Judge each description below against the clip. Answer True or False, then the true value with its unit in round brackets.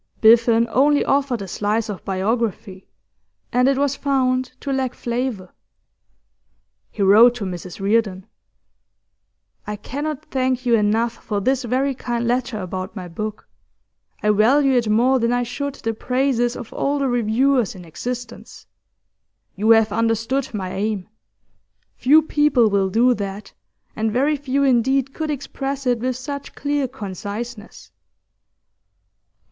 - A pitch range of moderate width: True (3.9 semitones)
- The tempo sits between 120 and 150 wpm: True (140 wpm)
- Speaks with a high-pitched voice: True (240 Hz)